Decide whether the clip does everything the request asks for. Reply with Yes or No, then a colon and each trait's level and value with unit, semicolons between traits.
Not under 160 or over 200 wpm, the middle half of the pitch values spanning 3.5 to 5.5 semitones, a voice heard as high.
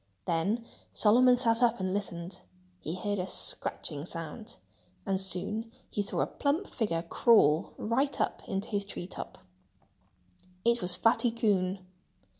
No: average, 140 wpm; average, 4.2 semitones; high, 205 Hz